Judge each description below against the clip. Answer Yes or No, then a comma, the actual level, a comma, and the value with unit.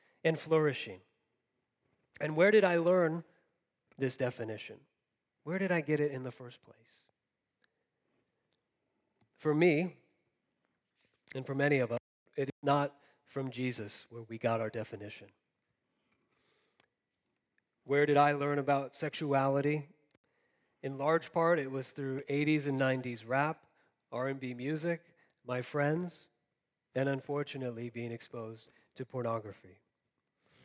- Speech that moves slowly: Yes, slow, 115 wpm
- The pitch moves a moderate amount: Yes, average, 3.7 semitones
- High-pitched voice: No, low, 135 Hz